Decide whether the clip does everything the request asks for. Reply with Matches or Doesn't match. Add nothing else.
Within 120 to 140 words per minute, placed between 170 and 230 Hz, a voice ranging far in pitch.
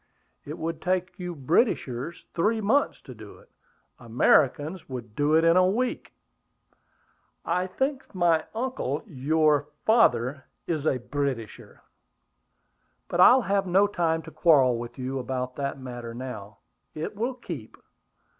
Doesn't match